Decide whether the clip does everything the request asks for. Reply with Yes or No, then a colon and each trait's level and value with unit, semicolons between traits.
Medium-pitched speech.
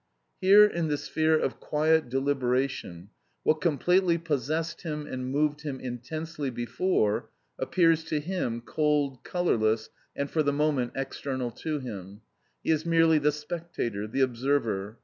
Yes: medium, 145 Hz